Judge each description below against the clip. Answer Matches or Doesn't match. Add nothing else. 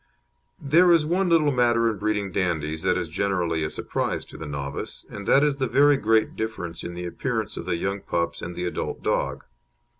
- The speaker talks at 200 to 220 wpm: Matches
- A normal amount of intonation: Doesn't match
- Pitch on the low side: Matches